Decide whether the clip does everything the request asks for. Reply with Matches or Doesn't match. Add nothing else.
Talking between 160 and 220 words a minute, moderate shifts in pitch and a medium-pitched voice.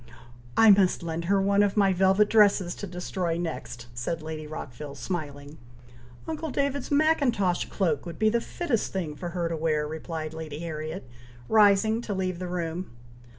Matches